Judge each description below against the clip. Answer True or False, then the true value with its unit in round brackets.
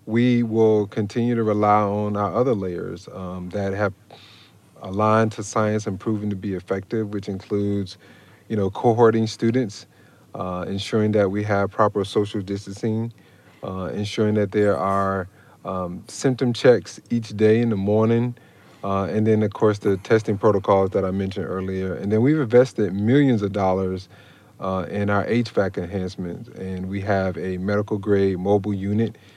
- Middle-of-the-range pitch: False (105 Hz)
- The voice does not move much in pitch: True (2.2 semitones)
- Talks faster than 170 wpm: False (160 wpm)